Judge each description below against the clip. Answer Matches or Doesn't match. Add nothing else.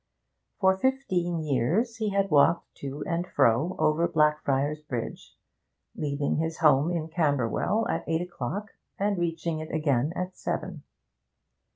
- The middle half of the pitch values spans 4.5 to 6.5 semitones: Doesn't match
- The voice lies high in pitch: Doesn't match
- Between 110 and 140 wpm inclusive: Matches